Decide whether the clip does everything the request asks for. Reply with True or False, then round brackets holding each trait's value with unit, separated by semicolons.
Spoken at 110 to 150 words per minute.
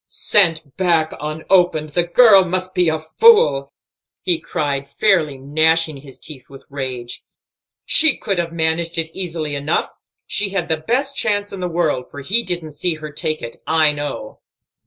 False (165 wpm)